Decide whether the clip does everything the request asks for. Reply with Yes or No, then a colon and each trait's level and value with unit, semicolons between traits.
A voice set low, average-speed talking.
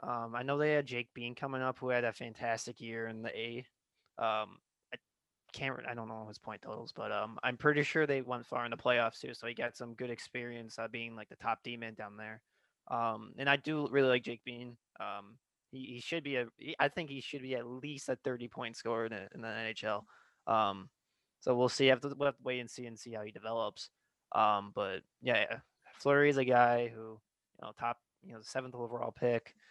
No: low, 120 Hz; fast, 230 wpm